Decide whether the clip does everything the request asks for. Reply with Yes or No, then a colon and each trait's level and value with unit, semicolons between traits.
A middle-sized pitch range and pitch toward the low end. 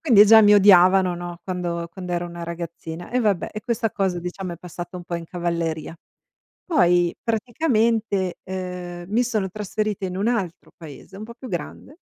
No: average, 3.6 semitones; medium, 185 Hz